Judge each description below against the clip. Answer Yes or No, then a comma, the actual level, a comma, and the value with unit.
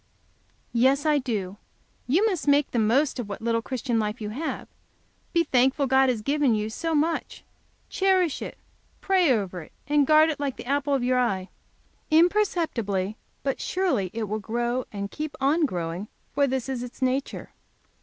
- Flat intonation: No, average, 5.3 semitones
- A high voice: Yes, very high, 260 Hz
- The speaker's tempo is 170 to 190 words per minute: Yes, average, 175 wpm